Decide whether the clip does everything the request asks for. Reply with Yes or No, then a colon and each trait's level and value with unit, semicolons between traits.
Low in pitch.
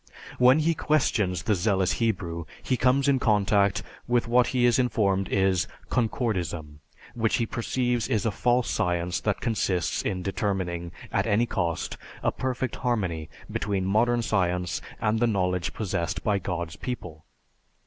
Yes: low, 105 Hz